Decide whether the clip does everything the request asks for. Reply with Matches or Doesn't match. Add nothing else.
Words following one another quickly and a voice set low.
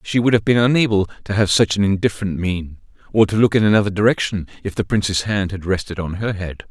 Matches